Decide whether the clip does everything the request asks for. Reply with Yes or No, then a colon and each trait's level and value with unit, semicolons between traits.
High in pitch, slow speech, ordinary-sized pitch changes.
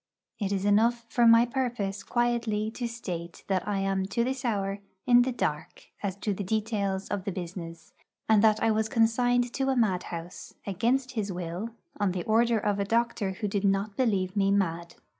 No: high, 210 Hz; average, 190 wpm; average, 3.4 semitones